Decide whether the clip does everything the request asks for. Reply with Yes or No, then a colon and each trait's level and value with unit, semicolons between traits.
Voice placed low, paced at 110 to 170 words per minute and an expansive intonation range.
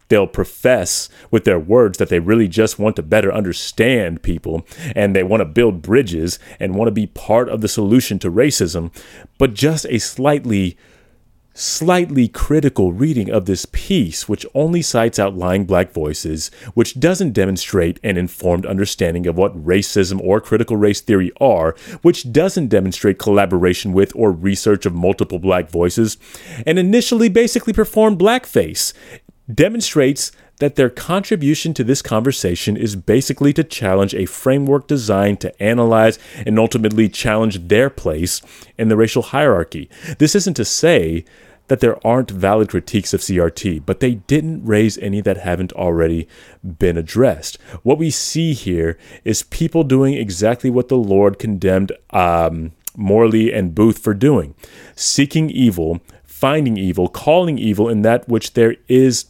Yes: low, 110 Hz; average, 155 wpm; wide, 6.0 semitones